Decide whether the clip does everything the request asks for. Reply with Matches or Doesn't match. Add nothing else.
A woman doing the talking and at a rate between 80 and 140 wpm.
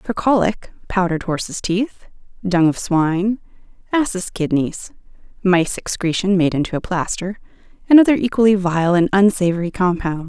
Matches